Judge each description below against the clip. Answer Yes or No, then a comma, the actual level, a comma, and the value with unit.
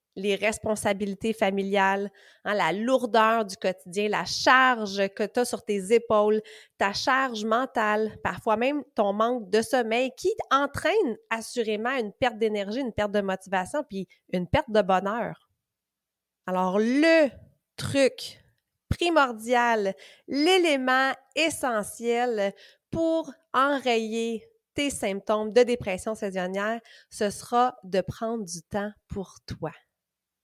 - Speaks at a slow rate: Yes, slow, 120 wpm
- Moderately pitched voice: No, high, 225 Hz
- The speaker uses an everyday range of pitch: Yes, average, 3.8 semitones